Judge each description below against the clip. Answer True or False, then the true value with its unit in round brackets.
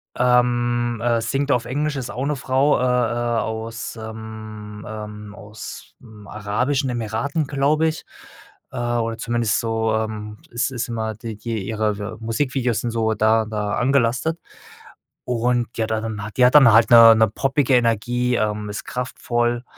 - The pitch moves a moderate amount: False (2.2 semitones)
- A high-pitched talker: False (115 Hz)